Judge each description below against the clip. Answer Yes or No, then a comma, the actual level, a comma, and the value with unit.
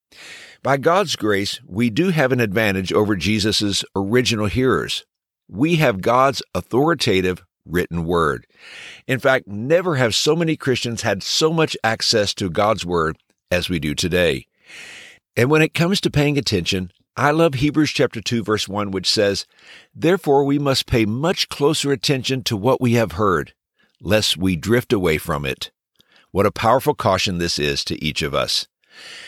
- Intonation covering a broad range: Yes, wide, 6.6 semitones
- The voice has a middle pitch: No, low, 110 Hz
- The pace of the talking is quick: No, average, 165 wpm